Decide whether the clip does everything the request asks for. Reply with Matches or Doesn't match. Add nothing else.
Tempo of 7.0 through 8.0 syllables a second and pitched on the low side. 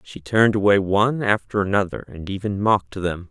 Doesn't match